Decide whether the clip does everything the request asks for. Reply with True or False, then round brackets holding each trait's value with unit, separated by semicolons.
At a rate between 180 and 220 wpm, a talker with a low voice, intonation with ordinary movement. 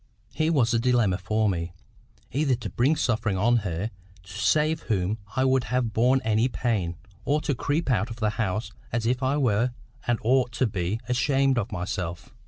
True (190 wpm; 115 Hz; 4.0 semitones)